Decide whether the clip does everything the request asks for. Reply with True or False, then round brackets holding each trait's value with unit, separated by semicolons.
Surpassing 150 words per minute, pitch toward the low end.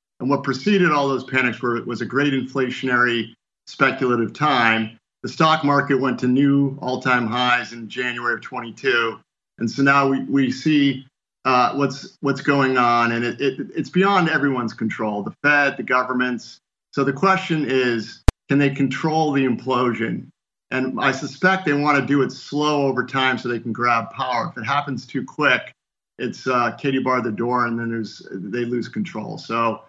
True (180 wpm; 130 Hz)